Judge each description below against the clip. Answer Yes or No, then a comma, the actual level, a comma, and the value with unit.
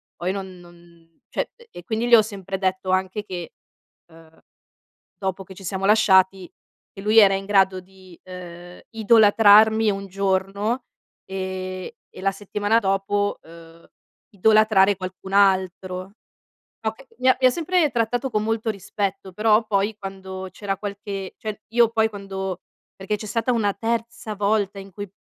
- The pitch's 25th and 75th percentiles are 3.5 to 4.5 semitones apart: No, narrow, 2.4 semitones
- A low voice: No, high, 195 Hz